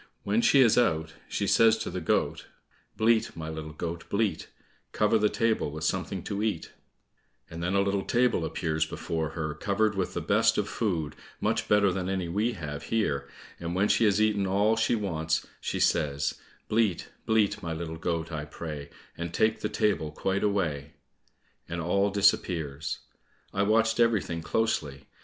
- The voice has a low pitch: Yes, very low, 95 Hz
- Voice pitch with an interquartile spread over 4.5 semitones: Yes, average, 5.0 semitones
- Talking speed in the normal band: Yes, average, 170 wpm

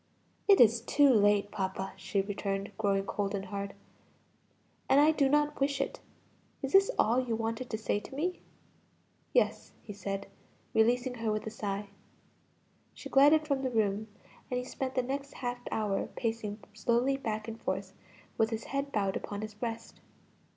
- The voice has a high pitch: Yes, high, 225 Hz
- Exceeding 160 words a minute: Yes, average, 170 wpm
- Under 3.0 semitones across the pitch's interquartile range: No, average, 4.7 semitones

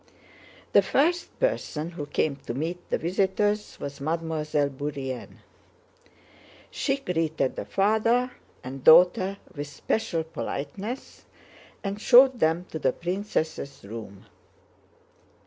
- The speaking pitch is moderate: Yes, medium, 165 Hz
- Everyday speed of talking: No, slow, 110 wpm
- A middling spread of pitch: No, wide, 6.3 semitones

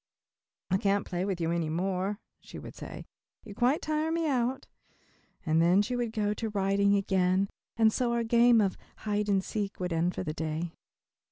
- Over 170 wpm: Yes, average, 190 wpm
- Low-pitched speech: No, high, 200 Hz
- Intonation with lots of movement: No, average, 4.2 semitones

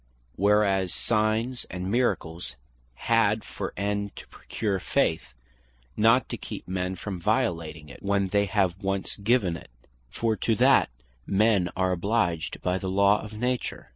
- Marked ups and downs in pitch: No, average, 3.2 semitones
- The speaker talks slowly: No, average, 145 wpm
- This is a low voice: Yes, low, 100 Hz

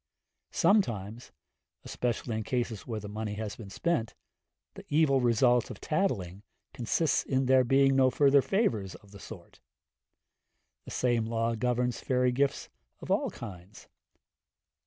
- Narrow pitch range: No, average, 3.6 semitones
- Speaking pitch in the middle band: No, low, 120 Hz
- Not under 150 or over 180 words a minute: No, slow, 135 wpm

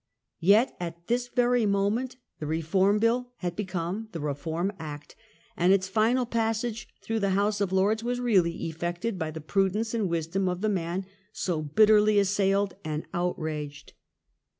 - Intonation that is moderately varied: Yes, average, 4.5 semitones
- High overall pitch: Yes, high, 195 Hz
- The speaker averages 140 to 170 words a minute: Yes, average, 155 wpm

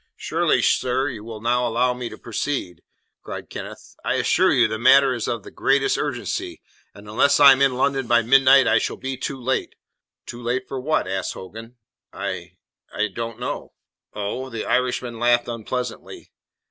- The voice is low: Yes, low, 125 Hz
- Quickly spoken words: No, average, 175 wpm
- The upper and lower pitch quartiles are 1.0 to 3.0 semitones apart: Yes, narrow, 2.5 semitones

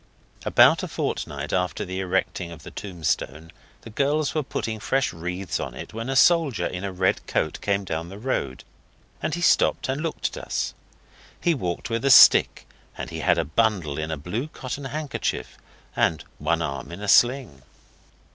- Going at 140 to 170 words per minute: No, average, 185 wpm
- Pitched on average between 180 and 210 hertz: No, low, 100 Hz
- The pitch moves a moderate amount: No, wide, 8.1 semitones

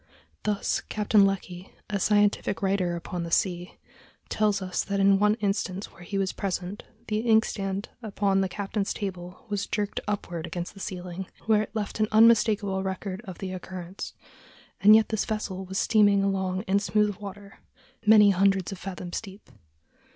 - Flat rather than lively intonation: Yes, narrow, 2.0 semitones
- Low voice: No, high, 195 Hz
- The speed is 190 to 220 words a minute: No, average, 165 wpm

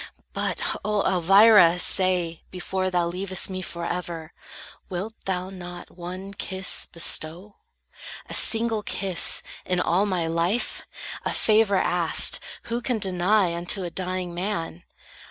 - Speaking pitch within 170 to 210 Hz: Yes, medium, 185 Hz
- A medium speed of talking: No, slow, 125 wpm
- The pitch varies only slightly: Yes, narrow, 2.3 semitones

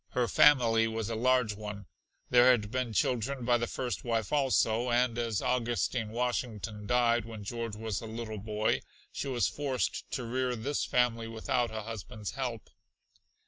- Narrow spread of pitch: Yes, narrow, 2.2 semitones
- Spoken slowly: No, average, 165 wpm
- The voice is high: No, low, 115 Hz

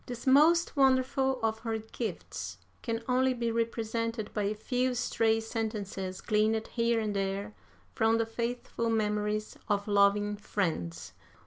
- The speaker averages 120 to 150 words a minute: Yes, slow, 135 wpm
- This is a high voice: Yes, high, 225 Hz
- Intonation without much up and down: Yes, narrow, 2.3 semitones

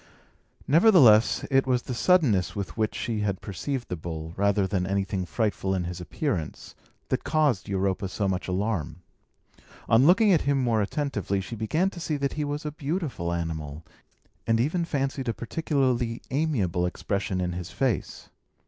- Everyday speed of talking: Yes, average, 165 wpm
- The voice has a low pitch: Yes, low, 110 Hz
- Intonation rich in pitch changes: Yes, wide, 7.1 semitones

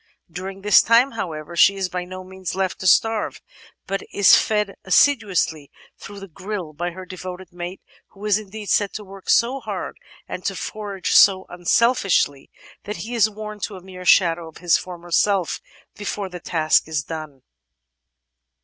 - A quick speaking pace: No, average, 170 wpm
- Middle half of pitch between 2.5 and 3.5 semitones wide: Yes, average, 2.9 semitones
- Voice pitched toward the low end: No, high, 190 Hz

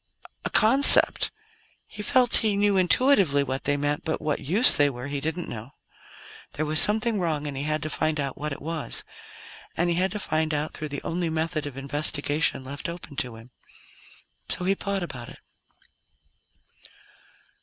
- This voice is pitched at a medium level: Yes, medium, 155 Hz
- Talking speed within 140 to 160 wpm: No, average, 175 wpm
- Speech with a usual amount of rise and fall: Yes, average, 4.1 semitones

